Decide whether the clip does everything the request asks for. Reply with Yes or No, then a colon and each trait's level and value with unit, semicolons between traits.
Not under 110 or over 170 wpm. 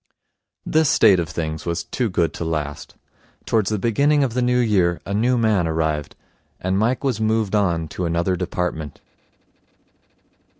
Yes: average, 160 wpm